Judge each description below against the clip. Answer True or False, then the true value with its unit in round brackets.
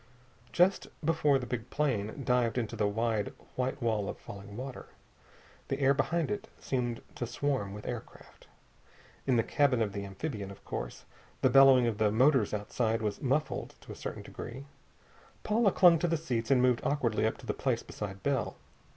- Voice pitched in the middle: False (125 Hz)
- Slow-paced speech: False (180 wpm)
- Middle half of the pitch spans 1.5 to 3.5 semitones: False (4.3 semitones)